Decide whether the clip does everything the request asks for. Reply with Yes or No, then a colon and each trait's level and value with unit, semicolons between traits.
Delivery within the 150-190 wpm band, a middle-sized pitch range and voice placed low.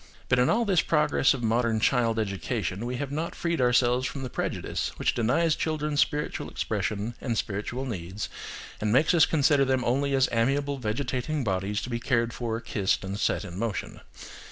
Yes: average, 180 wpm; average, 4.2 semitones; low, 125 Hz